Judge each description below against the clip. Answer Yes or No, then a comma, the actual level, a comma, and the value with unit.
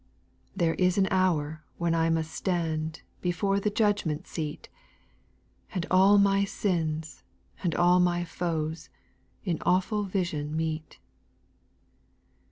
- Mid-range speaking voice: Yes, medium, 175 Hz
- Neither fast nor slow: No, slow, 120 wpm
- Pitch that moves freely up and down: No, average, 2.9 semitones